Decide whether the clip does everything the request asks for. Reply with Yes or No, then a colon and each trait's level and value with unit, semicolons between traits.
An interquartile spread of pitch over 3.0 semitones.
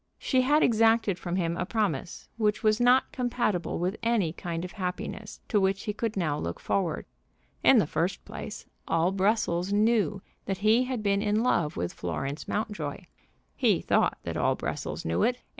Yes: average, 4.4 semitones